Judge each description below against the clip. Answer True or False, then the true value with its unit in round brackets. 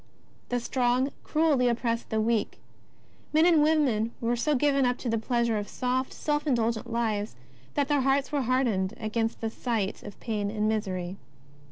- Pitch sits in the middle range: False (235 Hz)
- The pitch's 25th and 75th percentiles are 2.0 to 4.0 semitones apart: True (3.5 semitones)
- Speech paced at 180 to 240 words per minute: False (170 wpm)